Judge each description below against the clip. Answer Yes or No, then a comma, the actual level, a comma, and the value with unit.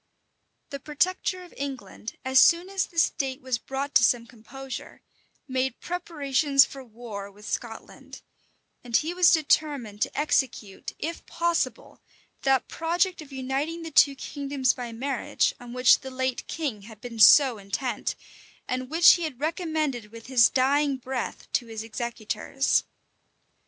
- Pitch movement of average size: Yes, average, 4.2 semitones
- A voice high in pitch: Yes, very high, 265 Hz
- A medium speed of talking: Yes, average, 145 wpm